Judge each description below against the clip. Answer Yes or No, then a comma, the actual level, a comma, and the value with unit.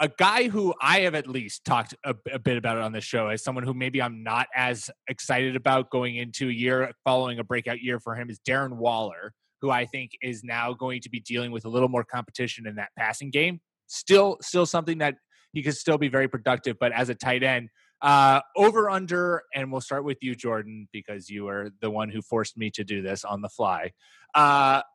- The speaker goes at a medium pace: No, fast, 225 wpm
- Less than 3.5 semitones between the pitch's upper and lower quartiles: Yes, average, 3.1 semitones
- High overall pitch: No, low, 125 Hz